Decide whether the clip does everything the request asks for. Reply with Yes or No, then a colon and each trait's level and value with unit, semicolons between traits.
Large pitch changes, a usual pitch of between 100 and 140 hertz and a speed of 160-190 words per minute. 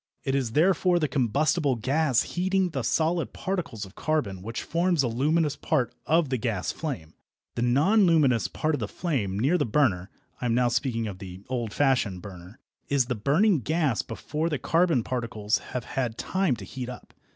Yes: wide, 5.8 semitones; low, 135 Hz; average, 185 wpm